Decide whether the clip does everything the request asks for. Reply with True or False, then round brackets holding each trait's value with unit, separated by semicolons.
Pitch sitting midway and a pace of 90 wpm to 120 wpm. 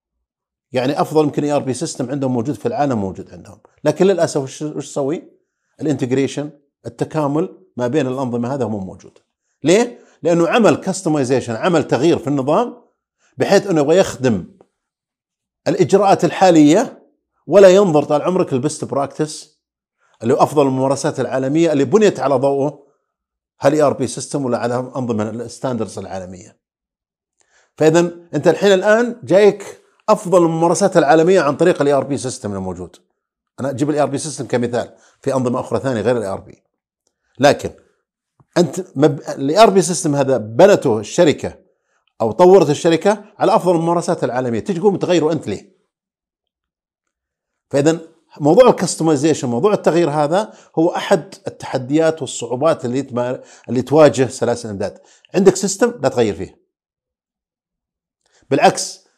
False (150 Hz; 135 wpm)